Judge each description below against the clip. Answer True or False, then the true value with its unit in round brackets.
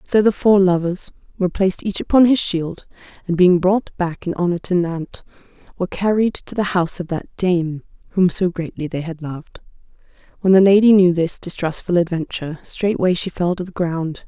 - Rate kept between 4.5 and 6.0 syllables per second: True (5.4 syllables/s)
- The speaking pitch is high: False (180 Hz)